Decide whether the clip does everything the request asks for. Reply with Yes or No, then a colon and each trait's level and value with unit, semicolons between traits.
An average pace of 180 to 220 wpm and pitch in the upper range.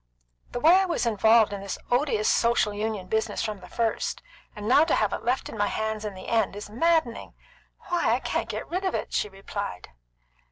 Yes: fast, 205 wpm; high, 220 Hz